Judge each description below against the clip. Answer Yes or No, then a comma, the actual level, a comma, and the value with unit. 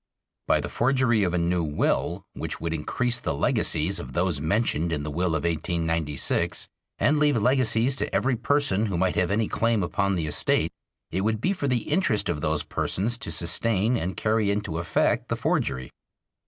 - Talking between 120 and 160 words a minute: No, average, 185 wpm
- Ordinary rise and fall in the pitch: No, wide, 6.1 semitones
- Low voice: Yes, very low, 95 Hz